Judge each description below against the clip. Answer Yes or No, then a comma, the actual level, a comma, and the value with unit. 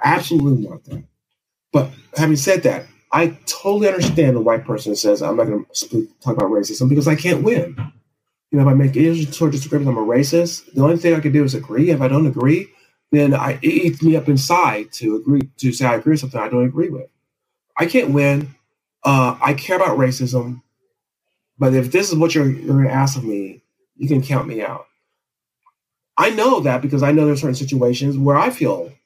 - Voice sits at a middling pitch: Yes, medium, 145 Hz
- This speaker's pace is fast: Yes, fast, 220 wpm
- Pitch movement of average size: Yes, average, 3.9 semitones